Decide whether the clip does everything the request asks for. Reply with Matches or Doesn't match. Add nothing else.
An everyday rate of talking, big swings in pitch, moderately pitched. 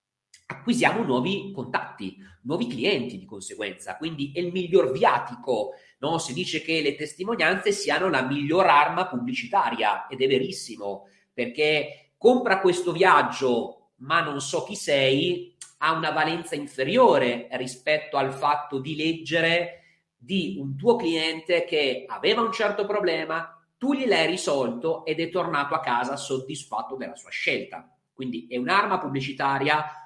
Doesn't match